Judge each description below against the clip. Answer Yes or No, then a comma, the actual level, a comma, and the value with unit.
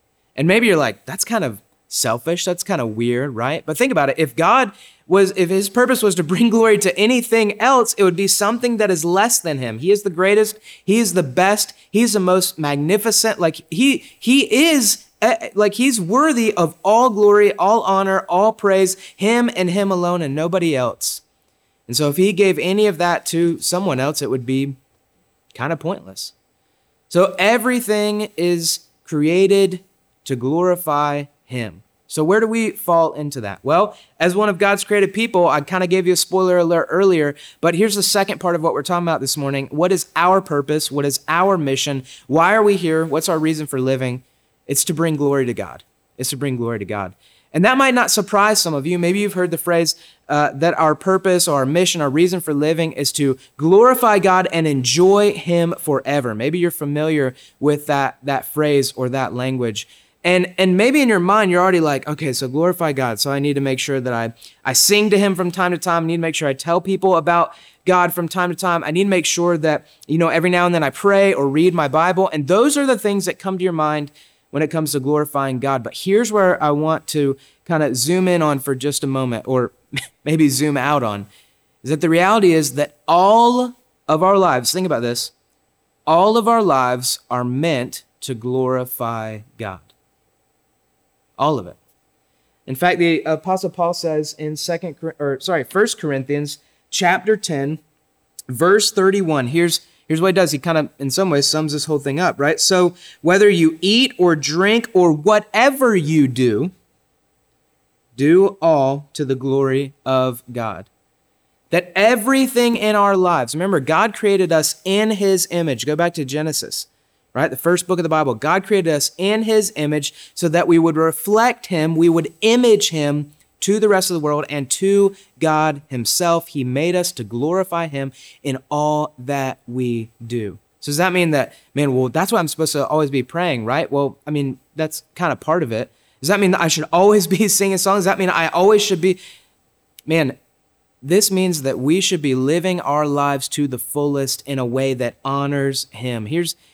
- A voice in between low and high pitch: Yes, medium, 165 Hz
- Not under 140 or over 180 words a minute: No, fast, 205 wpm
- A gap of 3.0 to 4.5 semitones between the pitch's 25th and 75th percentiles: No, average, 5.2 semitones